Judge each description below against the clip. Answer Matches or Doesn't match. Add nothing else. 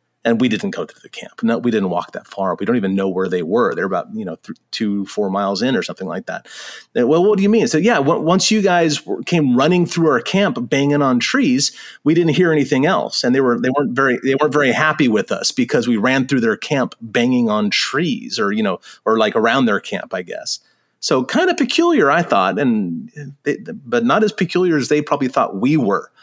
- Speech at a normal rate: Doesn't match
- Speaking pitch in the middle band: Matches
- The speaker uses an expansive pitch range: Matches